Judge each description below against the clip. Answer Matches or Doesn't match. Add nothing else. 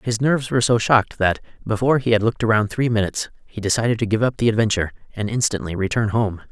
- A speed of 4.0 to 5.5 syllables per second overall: Doesn't match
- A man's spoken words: Matches